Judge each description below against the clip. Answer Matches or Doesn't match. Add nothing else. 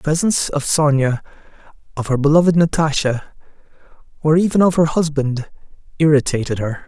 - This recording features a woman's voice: Doesn't match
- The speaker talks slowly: Matches